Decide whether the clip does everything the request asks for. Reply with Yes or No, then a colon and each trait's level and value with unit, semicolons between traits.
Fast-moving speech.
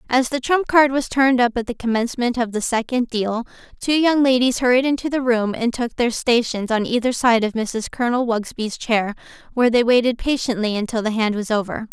Yes: fast, 210 wpm